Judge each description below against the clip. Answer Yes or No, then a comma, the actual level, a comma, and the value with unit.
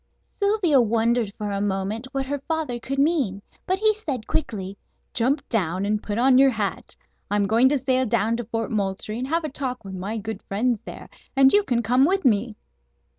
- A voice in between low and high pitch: No, high, 240 Hz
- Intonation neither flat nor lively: Yes, average, 4.7 semitones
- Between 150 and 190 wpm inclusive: No, average, 200 wpm